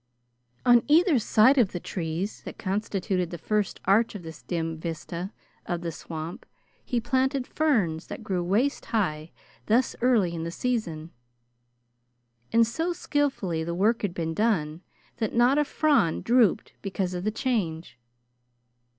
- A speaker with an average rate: Yes, average, 150 wpm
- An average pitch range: No, wide, 6.1 semitones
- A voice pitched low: No, high, 195 Hz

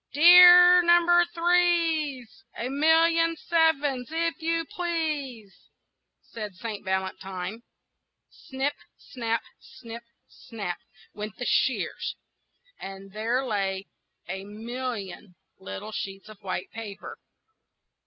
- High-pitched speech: Yes, very high, 250 Hz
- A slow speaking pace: Yes, slow, 95 wpm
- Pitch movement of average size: No, wide, 8.0 semitones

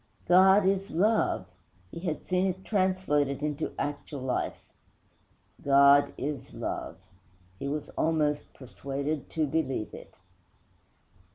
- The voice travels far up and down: No, average, 4.8 semitones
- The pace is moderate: No, slow, 110 wpm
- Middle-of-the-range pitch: Yes, medium, 150 Hz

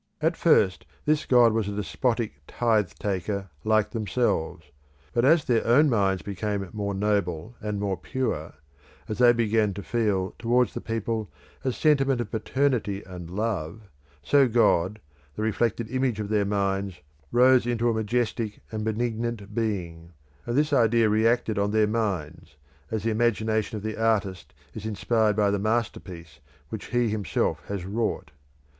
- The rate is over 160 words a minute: No, average, 155 wpm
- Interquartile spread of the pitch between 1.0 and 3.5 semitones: Yes, average, 2.9 semitones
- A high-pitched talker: No, low, 110 Hz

